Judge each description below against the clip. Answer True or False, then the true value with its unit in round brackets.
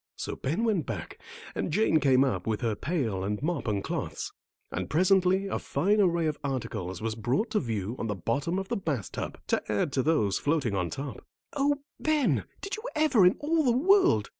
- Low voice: False (150 Hz)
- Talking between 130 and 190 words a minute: False (205 wpm)